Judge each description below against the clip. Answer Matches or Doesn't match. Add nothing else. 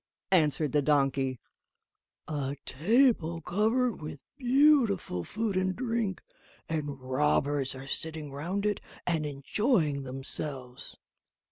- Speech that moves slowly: Matches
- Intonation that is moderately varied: Doesn't match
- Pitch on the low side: Doesn't match